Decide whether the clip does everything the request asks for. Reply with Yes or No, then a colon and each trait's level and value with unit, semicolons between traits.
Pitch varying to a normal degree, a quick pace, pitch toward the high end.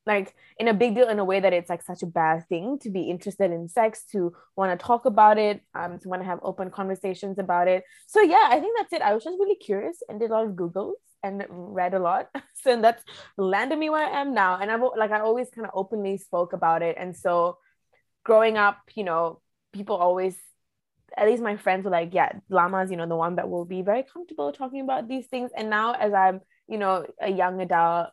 Yes: average, 4.2 semitones; fast, 245 wpm; high, 200 Hz